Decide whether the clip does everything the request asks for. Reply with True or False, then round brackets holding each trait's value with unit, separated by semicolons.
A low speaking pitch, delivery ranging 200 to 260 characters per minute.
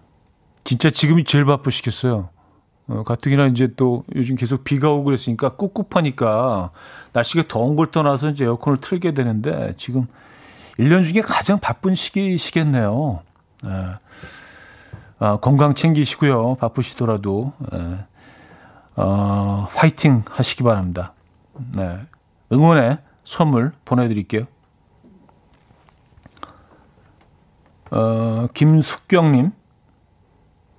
True (125 Hz; 230 characters per minute)